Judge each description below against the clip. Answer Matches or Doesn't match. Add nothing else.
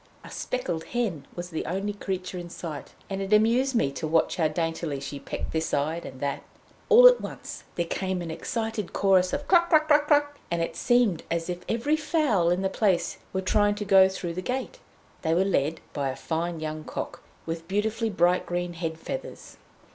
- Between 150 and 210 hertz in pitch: Matches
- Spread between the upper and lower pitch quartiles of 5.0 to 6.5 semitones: Matches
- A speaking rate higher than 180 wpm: Matches